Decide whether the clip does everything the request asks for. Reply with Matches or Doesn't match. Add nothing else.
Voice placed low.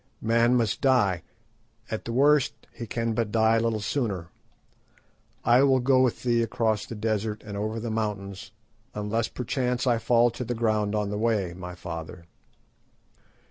Matches